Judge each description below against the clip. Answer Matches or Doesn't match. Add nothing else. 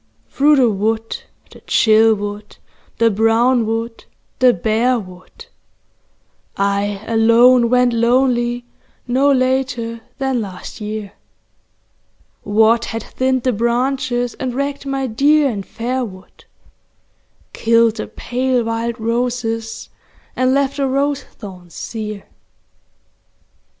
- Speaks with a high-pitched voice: Matches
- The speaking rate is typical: Doesn't match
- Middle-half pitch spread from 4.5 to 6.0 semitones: Doesn't match